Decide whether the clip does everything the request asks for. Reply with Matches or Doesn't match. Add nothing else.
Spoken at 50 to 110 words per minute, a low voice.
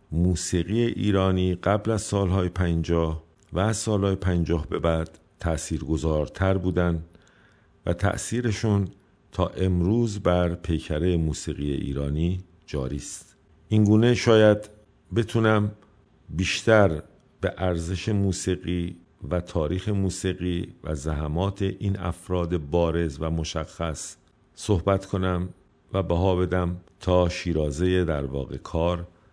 Matches